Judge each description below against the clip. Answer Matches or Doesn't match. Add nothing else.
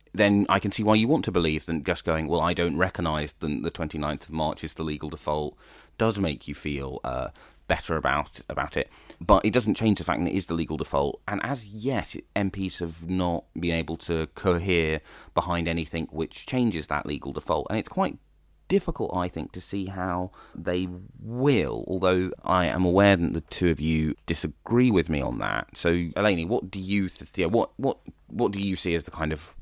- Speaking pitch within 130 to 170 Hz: Doesn't match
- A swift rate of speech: Matches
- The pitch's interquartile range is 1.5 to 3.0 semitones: Doesn't match